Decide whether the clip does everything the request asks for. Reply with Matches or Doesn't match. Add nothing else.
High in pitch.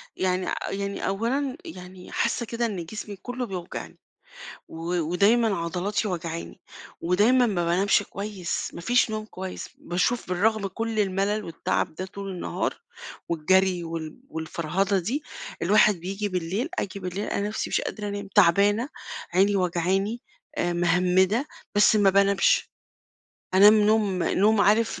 Matches